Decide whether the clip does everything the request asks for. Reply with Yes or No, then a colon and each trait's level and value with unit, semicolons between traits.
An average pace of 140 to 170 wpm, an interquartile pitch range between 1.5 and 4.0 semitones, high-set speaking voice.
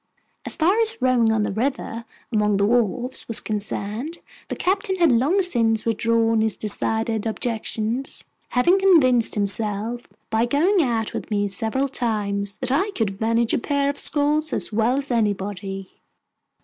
No: average, 155 wpm; average, 4.6 semitones; high, 230 Hz